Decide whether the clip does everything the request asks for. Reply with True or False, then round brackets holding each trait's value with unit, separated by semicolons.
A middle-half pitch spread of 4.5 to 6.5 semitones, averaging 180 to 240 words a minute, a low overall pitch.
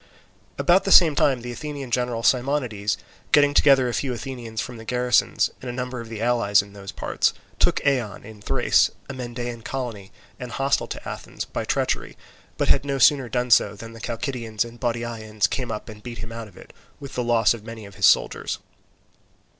False (2.5 semitones; 200 wpm; 120 Hz)